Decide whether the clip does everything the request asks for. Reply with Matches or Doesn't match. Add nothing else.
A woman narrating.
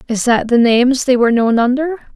Matches